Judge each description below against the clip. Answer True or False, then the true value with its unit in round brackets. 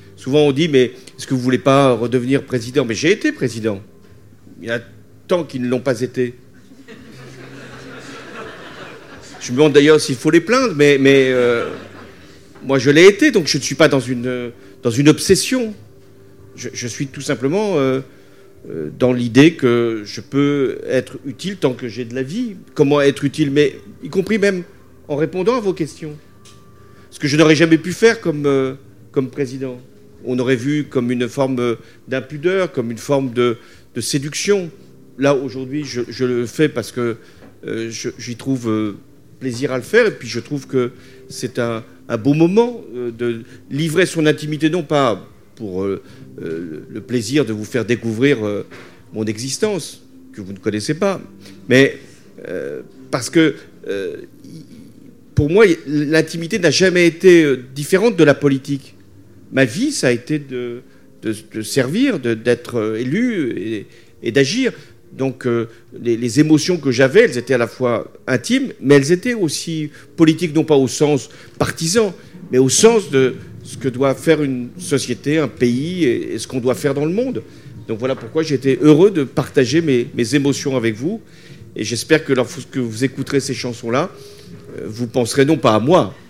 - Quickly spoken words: False (180 wpm)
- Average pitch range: True (4.5 semitones)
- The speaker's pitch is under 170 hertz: True (135 Hz)